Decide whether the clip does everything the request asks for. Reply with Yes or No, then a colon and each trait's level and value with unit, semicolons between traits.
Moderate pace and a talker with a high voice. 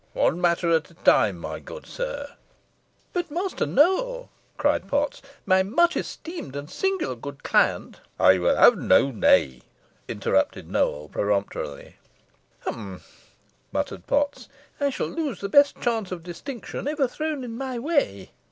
Yes: average, 145 wpm; high, 245 Hz